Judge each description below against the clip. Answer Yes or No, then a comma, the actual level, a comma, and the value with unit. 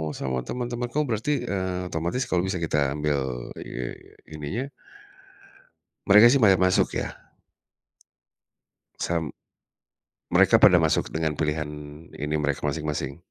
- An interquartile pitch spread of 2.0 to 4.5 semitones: No, wide, 5.6 semitones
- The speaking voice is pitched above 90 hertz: No, very low, 80 Hz